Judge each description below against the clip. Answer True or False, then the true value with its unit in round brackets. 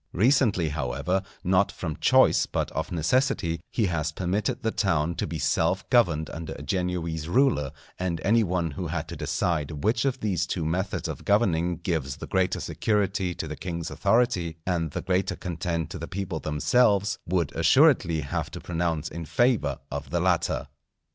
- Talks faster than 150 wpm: True (175 wpm)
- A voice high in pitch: False (85 Hz)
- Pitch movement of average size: True (3.4 semitones)